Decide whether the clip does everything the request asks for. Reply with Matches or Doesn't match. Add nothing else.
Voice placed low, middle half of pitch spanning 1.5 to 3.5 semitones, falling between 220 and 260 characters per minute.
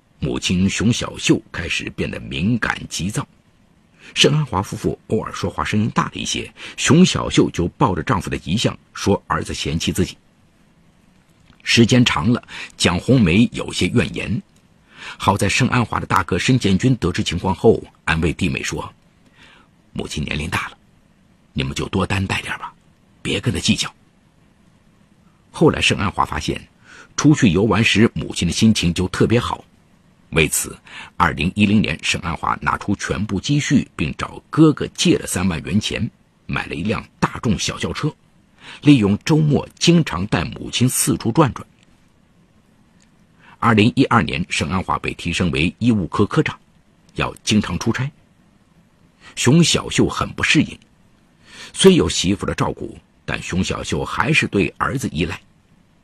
Doesn't match